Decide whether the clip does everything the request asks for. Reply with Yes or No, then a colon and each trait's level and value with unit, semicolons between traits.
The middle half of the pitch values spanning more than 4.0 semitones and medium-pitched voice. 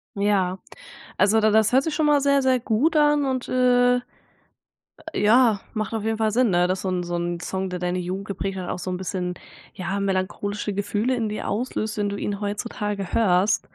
No: average, 4.5 semitones; high, 205 Hz